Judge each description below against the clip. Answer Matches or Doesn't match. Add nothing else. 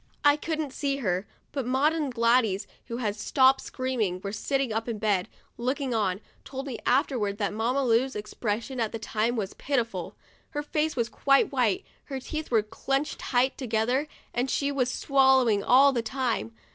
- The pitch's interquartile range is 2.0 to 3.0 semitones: Doesn't match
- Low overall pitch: Doesn't match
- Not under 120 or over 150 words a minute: Doesn't match